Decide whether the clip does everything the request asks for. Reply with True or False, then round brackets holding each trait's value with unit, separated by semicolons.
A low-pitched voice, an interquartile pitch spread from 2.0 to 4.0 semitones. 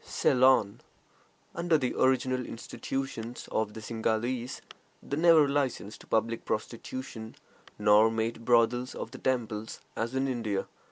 True (120 Hz; 2.8 semitones)